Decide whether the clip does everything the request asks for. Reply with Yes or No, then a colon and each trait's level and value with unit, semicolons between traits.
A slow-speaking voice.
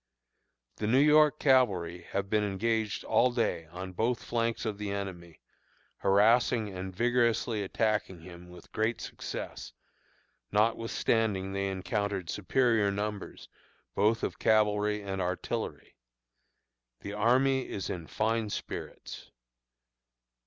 Yes: slow, 115 wpm